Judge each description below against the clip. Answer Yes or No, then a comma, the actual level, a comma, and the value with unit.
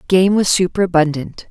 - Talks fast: No, slow, 120 wpm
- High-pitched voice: No, medium, 175 Hz